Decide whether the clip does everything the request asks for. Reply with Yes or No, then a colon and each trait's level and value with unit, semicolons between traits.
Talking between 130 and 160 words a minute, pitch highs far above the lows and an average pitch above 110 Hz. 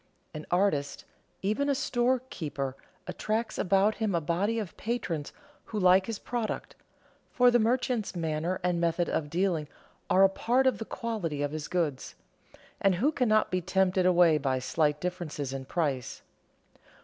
Yes: average, 155 wpm; wide, 5.8 semitones; medium, 185 Hz